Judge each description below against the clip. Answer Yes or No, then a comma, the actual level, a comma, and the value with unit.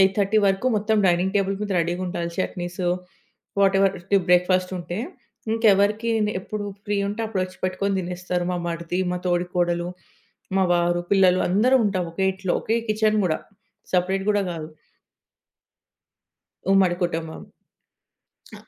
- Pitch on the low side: No, medium, 185 Hz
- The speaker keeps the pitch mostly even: Yes, narrow, 2.3 semitones